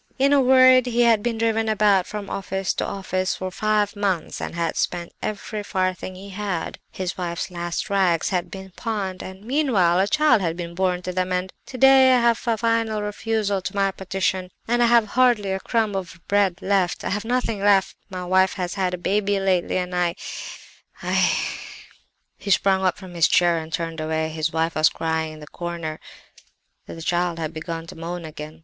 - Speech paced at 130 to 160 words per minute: No, average, 195 wpm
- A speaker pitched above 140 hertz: Yes, high, 190 Hz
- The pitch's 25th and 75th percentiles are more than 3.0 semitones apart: Yes, average, 3.5 semitones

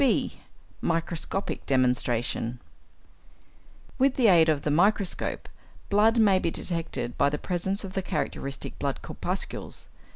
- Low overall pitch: No, medium, 170 Hz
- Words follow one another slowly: Yes, slow, 125 wpm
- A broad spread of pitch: Yes, wide, 5.9 semitones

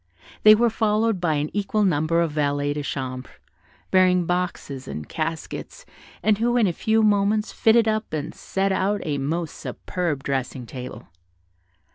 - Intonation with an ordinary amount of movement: No, wide, 6.5 semitones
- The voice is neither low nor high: Yes, medium, 175 Hz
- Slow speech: No, average, 155 wpm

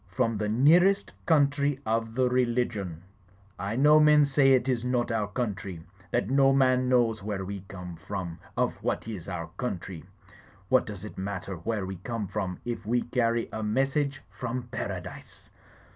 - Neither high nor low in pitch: No, low, 115 Hz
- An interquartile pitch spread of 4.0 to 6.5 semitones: Yes, average, 4.6 semitones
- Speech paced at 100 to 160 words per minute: No, average, 170 wpm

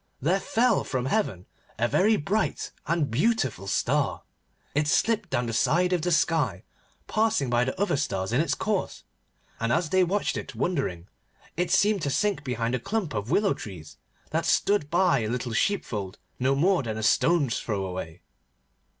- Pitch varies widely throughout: Yes, wide, 8.5 semitones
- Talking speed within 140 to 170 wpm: No, average, 185 wpm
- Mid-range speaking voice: Yes, medium, 145 Hz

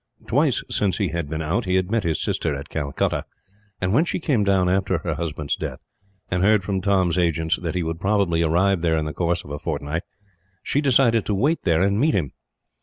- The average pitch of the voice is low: Yes, very low, 90 Hz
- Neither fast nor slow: No, fast, 220 wpm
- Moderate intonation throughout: Yes, average, 3.5 semitones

